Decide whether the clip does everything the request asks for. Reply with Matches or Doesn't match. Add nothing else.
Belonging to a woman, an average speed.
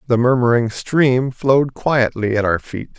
Doesn't match